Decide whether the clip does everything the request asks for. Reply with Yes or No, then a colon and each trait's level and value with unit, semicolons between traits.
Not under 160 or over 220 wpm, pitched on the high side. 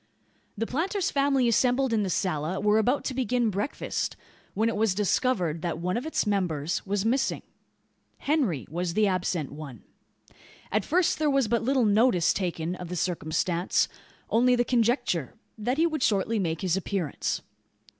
Yes: average, 165 wpm; high, 210 Hz